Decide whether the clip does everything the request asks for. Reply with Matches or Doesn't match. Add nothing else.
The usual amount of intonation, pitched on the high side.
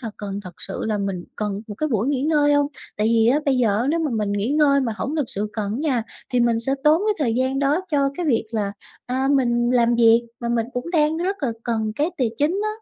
Matches